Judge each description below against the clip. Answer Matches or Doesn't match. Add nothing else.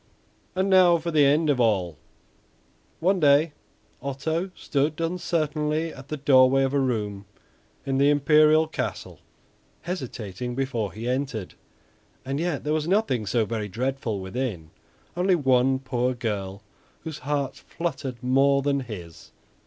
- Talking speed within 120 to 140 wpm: Matches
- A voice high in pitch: Doesn't match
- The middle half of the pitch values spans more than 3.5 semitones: Matches